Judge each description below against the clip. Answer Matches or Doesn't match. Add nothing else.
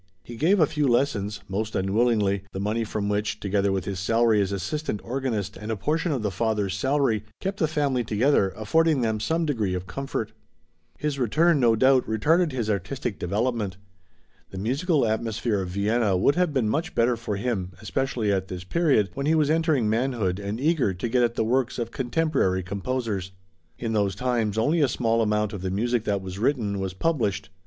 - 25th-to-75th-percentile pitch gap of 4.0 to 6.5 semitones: Matches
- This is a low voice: Matches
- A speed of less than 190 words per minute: Doesn't match